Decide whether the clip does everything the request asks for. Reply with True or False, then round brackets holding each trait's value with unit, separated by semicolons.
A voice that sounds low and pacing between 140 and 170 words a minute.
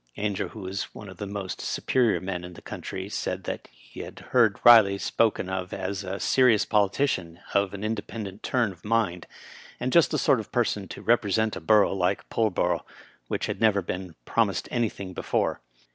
False (100 Hz; 190 wpm)